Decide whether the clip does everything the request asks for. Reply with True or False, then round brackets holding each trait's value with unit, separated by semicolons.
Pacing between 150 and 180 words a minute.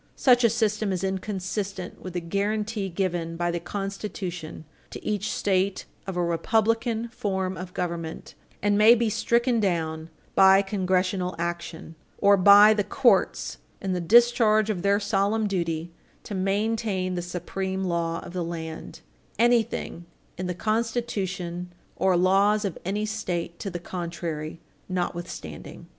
False (140 wpm)